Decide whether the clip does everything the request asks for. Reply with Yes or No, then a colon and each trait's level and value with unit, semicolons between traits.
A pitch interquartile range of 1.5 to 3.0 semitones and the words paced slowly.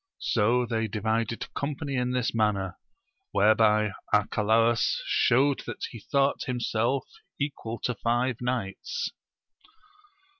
Yes: average, 2.7 semitones; slow, 105 wpm